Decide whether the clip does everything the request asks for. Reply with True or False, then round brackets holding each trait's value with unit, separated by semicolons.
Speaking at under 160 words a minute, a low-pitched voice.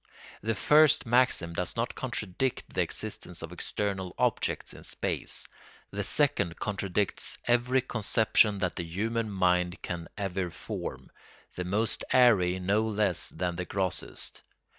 True (135 wpm; 100 Hz)